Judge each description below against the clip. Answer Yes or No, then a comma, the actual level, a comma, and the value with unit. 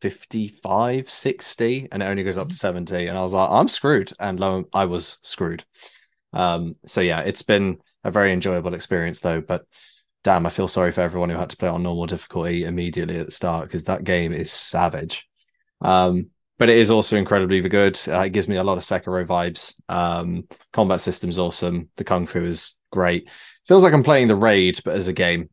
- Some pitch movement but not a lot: No, narrow, 1.9 semitones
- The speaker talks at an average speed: No, fast, 210 wpm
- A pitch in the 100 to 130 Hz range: No, very low, 90 Hz